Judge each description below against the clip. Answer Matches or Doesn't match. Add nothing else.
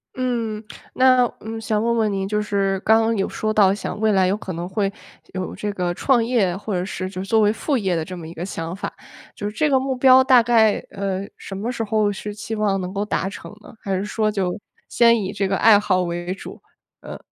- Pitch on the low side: Doesn't match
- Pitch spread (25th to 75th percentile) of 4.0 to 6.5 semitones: Doesn't match